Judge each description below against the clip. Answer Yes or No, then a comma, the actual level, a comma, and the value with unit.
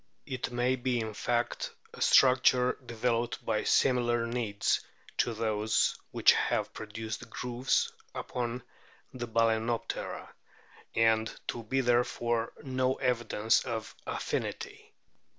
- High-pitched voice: No, low, 120 Hz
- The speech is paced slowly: Yes, slow, 115 wpm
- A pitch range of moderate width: No, narrow, 1.8 semitones